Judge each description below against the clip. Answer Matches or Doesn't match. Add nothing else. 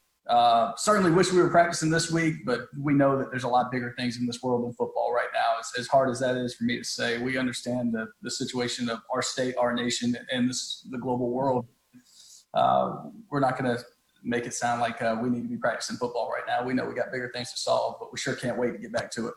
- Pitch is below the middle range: Matches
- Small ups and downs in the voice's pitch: Matches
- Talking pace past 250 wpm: Matches